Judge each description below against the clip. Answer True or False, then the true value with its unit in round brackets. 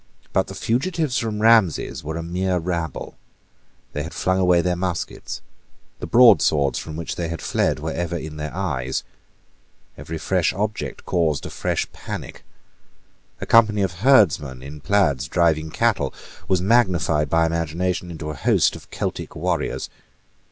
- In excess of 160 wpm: False (150 wpm)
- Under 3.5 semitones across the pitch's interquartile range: False (3.9 semitones)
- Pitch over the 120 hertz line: False (85 Hz)